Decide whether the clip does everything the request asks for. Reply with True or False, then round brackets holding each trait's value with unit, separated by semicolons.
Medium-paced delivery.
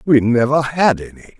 True (175 wpm)